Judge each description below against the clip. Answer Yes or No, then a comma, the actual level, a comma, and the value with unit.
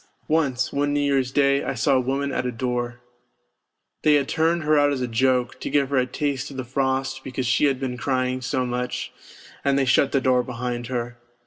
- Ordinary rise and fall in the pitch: No, narrow, 2.0 semitones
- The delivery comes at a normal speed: No, fast, 220 wpm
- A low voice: Yes, low, 130 Hz